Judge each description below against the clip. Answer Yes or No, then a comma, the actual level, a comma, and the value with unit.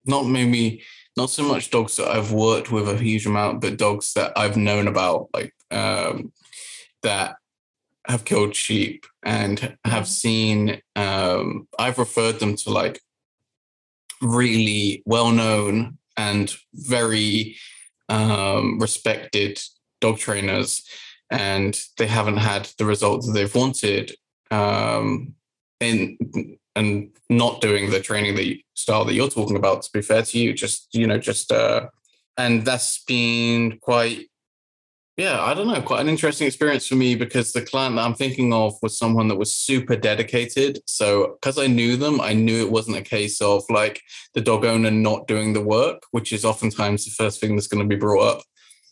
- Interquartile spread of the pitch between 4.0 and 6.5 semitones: No, average, 2.8 semitones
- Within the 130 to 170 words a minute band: Yes, average, 165 wpm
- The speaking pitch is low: Yes, low, 110 Hz